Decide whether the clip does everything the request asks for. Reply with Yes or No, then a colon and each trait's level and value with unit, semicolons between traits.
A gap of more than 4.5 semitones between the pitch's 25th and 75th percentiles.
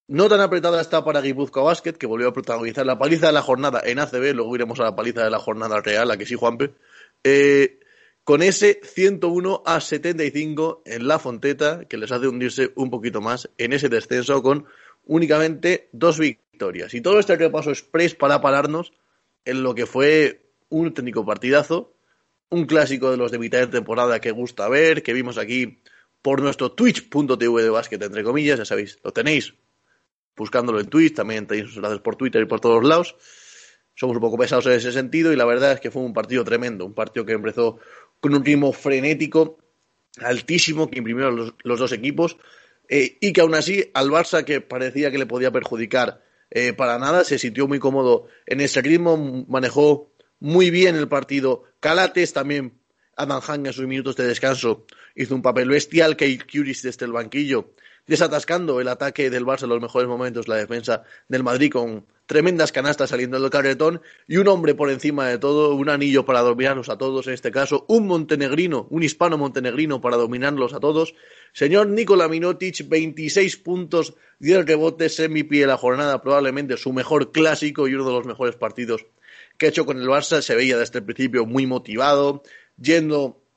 No: average, 4.2 semitones